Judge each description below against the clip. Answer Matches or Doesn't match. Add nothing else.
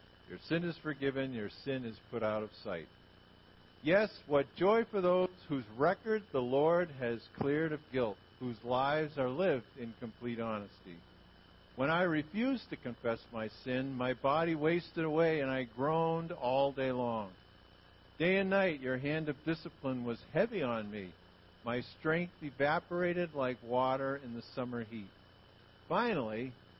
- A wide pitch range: Matches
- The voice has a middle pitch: Doesn't match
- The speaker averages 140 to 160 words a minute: Matches